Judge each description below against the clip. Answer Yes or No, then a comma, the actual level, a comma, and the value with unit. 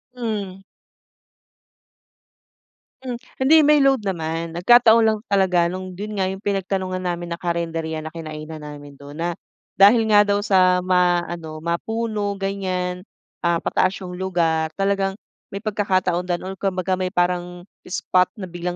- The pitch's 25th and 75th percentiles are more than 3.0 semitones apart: No, narrow, 2.6 semitones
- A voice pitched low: No, medium, 185 Hz